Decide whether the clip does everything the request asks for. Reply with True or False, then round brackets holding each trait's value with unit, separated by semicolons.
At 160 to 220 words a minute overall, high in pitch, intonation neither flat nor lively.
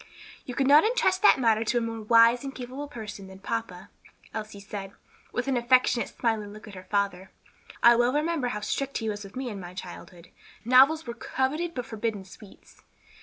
True (195 wpm; 230 Hz; 4.2 semitones)